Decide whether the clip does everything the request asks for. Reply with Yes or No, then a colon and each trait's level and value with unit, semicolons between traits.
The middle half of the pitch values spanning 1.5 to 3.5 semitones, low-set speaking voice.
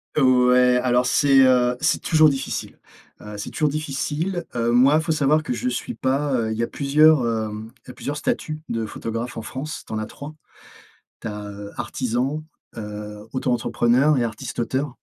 No: average, 4.0 semitones; low, 125 Hz